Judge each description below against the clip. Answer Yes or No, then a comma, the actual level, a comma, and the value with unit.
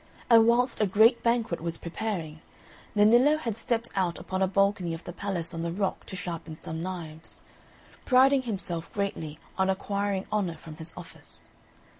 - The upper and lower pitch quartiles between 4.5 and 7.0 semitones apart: Yes, average, 4.8 semitones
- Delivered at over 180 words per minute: No, average, 165 wpm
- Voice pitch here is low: No, high, 190 Hz